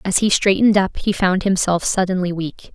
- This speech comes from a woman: Yes, female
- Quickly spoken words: No, average, 195 wpm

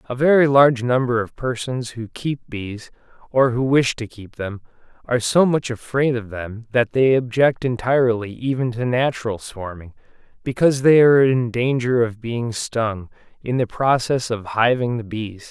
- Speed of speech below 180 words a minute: Yes, average, 170 wpm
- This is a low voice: Yes, low, 120 Hz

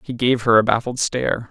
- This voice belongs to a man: Yes, male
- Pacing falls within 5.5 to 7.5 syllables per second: Yes, 5.7 syllables/s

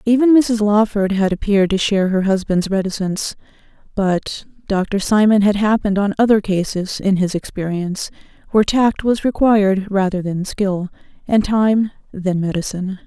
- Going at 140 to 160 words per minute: Yes, average, 145 wpm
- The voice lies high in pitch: Yes, high, 200 Hz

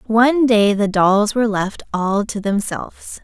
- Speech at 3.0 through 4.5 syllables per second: Yes, 4.4 syllables/s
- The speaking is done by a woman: Yes, female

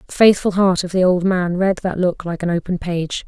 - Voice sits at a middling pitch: Yes, medium, 180 Hz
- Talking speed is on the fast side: Yes, fast, 255 wpm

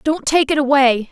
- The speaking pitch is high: Yes, very high, 280 Hz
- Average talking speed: No, fast, 215 wpm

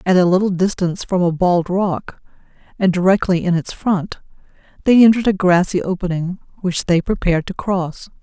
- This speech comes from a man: No, female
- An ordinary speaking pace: Yes, average, 170 wpm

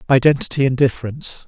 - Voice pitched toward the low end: Yes, low, 130 Hz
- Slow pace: Yes, slow, 120 wpm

